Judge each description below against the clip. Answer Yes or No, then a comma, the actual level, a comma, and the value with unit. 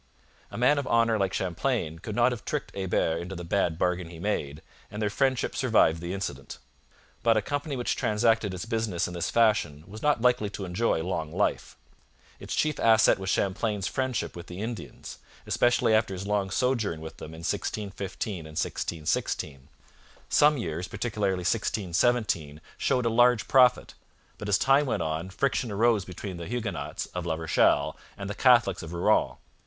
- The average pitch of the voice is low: Yes, low, 100 Hz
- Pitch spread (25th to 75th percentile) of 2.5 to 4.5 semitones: No, average, 5.2 semitones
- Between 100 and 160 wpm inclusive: No, average, 175 wpm